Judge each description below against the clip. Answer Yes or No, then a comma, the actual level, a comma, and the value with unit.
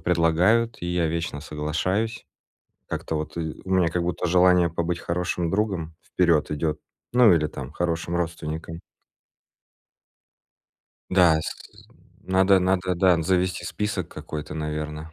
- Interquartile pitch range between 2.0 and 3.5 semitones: Yes, narrow, 2.5 semitones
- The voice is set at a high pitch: No, very low, 85 Hz